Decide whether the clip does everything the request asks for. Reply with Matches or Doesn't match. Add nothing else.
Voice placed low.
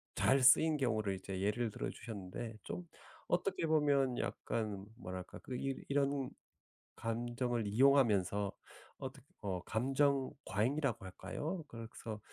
Matches